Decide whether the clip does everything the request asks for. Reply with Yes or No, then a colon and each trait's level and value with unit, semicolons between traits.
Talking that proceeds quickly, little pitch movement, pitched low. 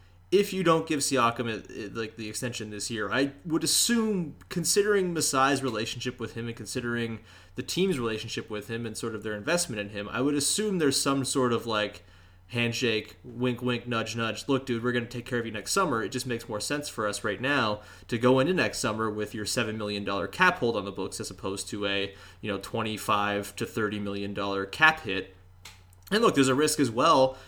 No: fast, 225 wpm; average, 4.3 semitones; low, 115 Hz